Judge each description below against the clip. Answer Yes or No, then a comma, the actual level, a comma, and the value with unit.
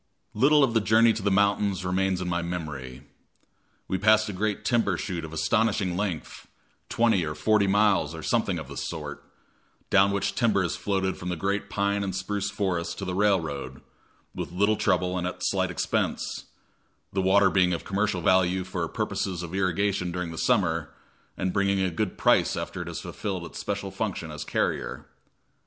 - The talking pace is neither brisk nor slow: Yes, average, 180 wpm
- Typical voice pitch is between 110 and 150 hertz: No, very low, 95 Hz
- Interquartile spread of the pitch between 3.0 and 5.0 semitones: No, narrow, 2.5 semitones